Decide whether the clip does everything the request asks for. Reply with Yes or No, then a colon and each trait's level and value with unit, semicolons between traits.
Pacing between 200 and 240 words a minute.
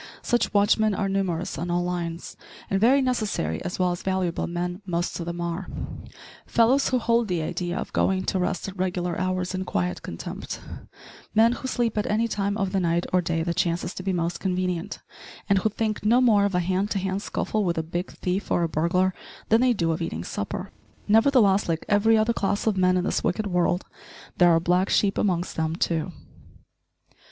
Yes: fast, 205 wpm